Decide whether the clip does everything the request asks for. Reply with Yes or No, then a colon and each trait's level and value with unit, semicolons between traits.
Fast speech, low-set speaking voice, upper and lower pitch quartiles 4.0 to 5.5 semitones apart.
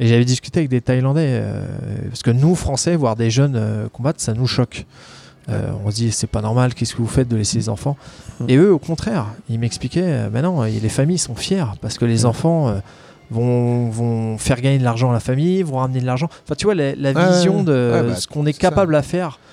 Yes: fast, 245 wpm; low, 125 Hz; average, 4.4 semitones